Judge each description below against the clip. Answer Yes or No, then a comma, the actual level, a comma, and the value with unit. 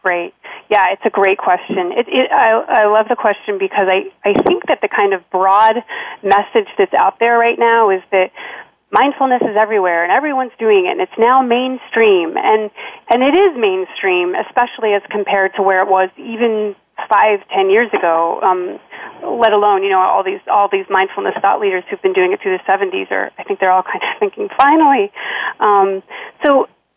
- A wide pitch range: Yes, wide, 6.5 semitones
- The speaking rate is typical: Yes, average, 195 wpm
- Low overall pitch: No, high, 215 Hz